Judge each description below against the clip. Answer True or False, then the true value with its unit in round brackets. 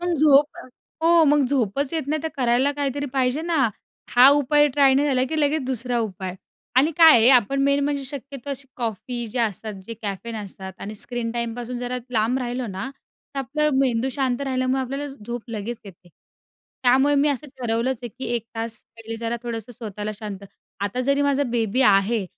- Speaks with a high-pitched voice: True (250 Hz)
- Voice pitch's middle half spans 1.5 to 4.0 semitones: True (3.5 semitones)